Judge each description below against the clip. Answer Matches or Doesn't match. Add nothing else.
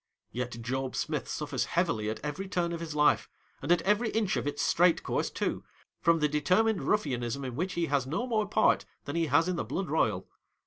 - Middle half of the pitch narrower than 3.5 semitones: Doesn't match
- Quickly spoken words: Matches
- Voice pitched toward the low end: Doesn't match